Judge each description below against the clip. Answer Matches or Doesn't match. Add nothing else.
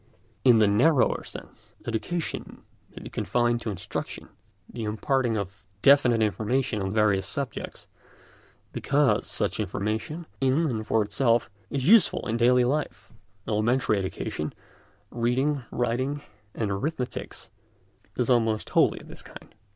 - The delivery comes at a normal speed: Doesn't match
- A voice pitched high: Doesn't match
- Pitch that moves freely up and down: Doesn't match